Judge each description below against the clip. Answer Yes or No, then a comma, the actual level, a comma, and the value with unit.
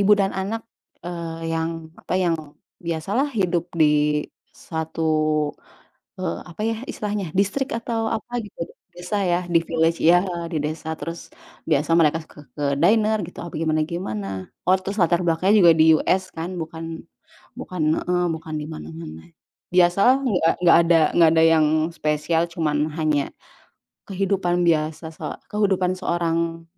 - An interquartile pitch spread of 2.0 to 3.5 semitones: Yes, average, 2.7 semitones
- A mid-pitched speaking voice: Yes, medium, 170 Hz